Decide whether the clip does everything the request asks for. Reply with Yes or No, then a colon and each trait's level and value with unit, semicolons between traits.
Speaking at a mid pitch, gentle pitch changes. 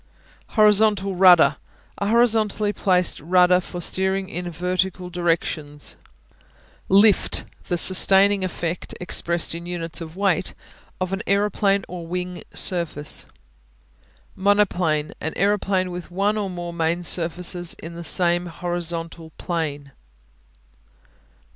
Yes: medium, 180 Hz; narrow, 2.3 semitones